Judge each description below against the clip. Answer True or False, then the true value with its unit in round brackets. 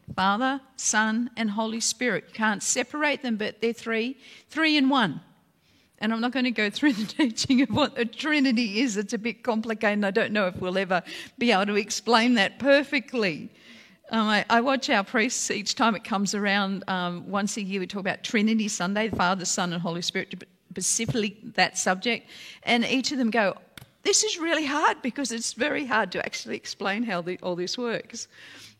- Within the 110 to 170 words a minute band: False (195 wpm)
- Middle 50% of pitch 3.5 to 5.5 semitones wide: True (4.0 semitones)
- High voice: True (225 Hz)